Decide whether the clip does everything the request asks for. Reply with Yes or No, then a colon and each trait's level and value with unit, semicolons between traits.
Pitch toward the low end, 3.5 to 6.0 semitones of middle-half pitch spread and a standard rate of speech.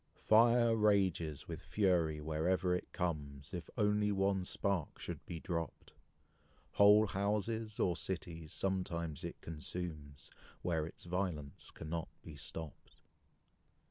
No: very low, 90 Hz; average, 4.1 semitones; slow, 115 wpm